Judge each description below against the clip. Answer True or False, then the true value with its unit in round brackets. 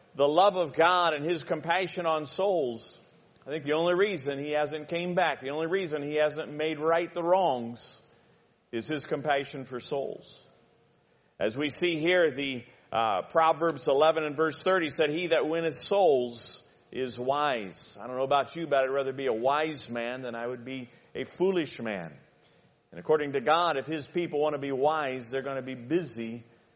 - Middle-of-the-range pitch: True (150 Hz)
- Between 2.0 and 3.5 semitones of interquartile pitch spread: False (4.1 semitones)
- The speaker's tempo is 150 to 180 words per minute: False (190 wpm)